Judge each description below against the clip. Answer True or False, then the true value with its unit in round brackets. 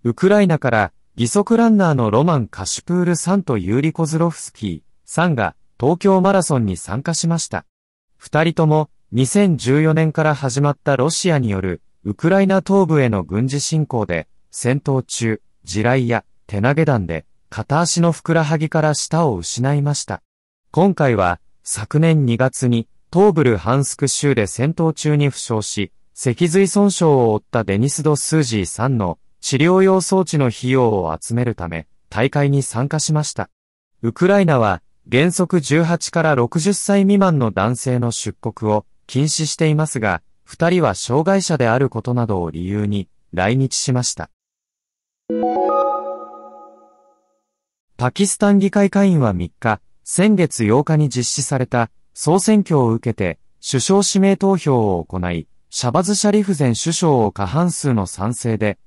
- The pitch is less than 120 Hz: False (135 Hz)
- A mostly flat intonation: False (7.1 semitones)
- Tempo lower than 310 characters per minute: True (290 characters per minute)